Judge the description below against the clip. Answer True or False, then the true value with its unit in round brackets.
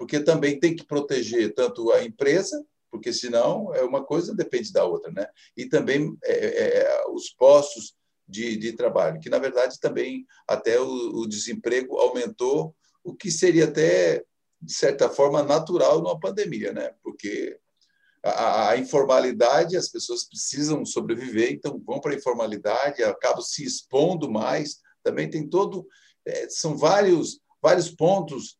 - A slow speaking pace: False (135 wpm)